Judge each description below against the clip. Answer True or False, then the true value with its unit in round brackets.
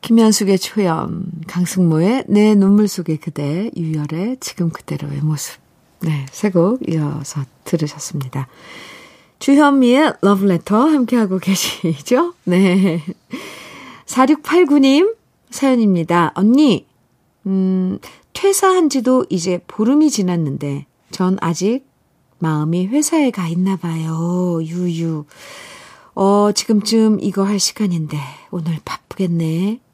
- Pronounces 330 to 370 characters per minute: False (225 characters per minute)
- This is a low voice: False (185 Hz)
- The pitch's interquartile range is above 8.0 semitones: False (5.5 semitones)